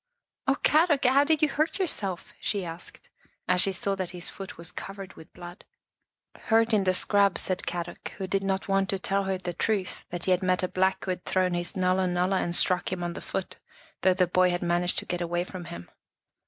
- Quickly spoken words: Yes, fast, 235 wpm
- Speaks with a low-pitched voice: No, medium, 185 Hz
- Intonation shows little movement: Yes, narrow, 1.8 semitones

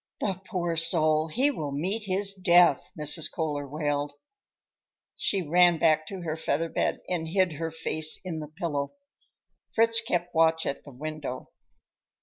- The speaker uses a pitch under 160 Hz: No, medium, 165 Hz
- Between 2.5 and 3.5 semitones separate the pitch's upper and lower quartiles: Yes, average, 2.9 semitones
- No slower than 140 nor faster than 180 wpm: Yes, average, 150 wpm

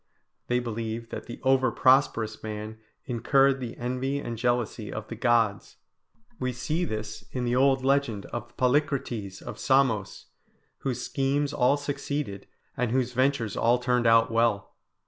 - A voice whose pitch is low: Yes, low, 125 Hz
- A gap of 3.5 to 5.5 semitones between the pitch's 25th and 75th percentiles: No, average, 2.9 semitones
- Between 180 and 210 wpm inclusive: No, average, 145 wpm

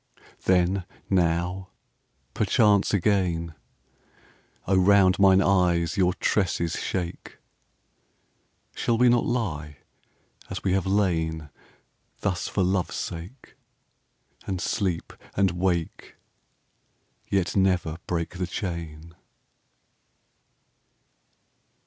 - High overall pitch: No, very low, 90 Hz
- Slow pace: Yes, slow, 90 wpm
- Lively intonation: No, narrow, 2.5 semitones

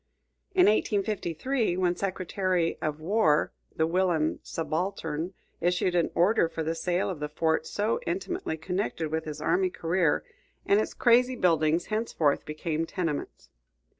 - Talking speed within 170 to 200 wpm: No, slow, 135 wpm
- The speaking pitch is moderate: Yes, medium, 175 Hz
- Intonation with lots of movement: No, average, 4.0 semitones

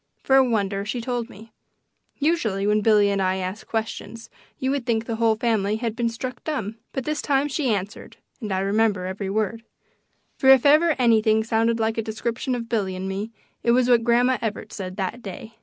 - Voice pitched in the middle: No, high, 225 Hz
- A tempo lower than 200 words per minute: No, fast, 205 wpm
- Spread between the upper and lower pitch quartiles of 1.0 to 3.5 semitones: Yes, average, 3.0 semitones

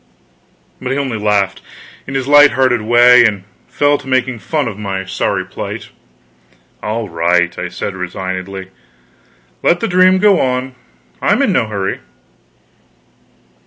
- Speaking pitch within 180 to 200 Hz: No, low, 115 Hz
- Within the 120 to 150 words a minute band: Yes, average, 140 wpm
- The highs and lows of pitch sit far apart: Yes, wide, 5.7 semitones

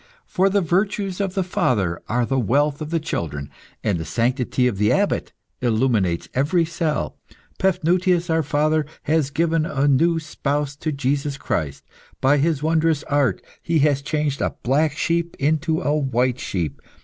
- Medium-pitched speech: Yes, medium, 145 Hz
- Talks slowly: No, average, 160 wpm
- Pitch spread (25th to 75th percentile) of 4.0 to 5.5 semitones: Yes, average, 4.3 semitones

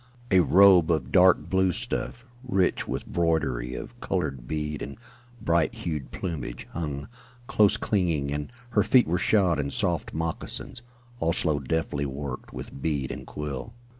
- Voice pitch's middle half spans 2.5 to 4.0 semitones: No, average, 4.6 semitones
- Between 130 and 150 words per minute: Yes, average, 145 wpm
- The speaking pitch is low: Yes, very low, 80 Hz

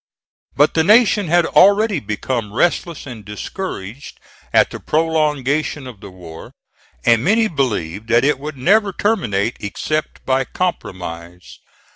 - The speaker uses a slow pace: Yes, slow, 130 wpm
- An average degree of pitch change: No, wide, 8.7 semitones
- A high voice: No, low, 135 Hz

